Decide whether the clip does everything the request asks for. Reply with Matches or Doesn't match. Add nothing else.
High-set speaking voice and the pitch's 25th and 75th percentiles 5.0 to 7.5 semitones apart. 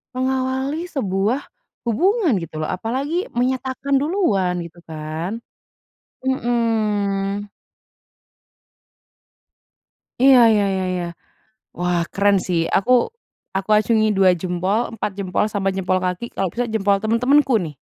Matches